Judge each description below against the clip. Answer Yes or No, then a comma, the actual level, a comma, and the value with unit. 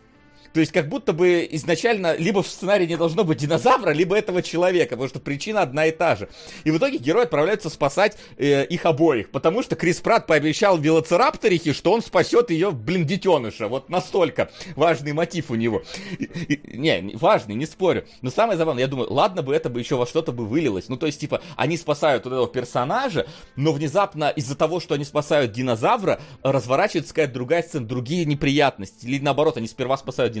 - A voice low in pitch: No, medium, 160 Hz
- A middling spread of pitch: Yes, average, 3.7 semitones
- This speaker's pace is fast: Yes, fast, 195 wpm